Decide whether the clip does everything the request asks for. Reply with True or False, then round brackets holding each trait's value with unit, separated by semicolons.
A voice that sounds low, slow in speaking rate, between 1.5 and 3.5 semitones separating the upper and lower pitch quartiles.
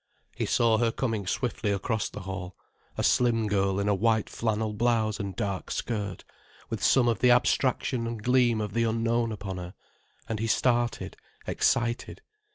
False (110 Hz; 165 wpm; 2.6 semitones)